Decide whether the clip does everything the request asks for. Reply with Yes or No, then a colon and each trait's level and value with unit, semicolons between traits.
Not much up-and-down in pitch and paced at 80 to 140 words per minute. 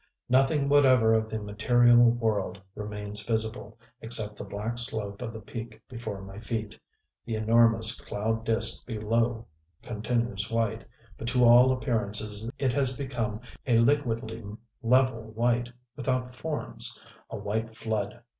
Yes: narrow, 1.9 semitones; slow, 135 wpm